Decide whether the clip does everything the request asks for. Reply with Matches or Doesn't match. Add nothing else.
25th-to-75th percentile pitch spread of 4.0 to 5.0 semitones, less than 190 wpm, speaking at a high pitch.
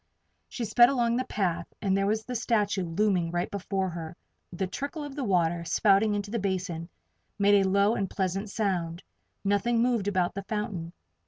Doesn't match